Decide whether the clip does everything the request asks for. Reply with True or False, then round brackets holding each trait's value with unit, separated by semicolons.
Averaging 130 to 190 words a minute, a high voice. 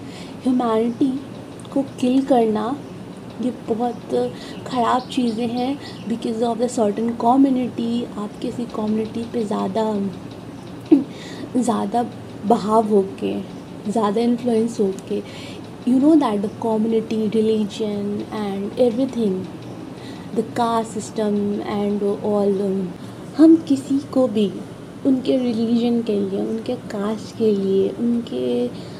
False (110 wpm; 230 Hz)